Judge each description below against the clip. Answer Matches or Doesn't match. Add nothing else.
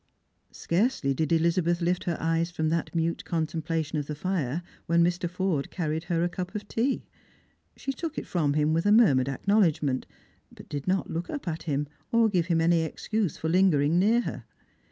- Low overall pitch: Doesn't match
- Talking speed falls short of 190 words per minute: Doesn't match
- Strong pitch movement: Doesn't match